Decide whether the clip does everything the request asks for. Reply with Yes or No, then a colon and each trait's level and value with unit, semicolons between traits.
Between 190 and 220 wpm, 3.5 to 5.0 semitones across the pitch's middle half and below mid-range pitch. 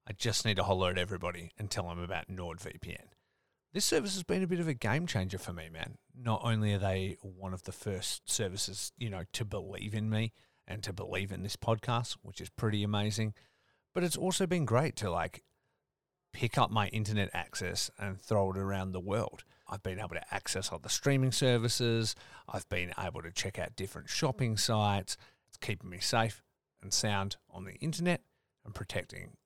Yes: average, 200 wpm; average, 4.0 semitones; low, 105 Hz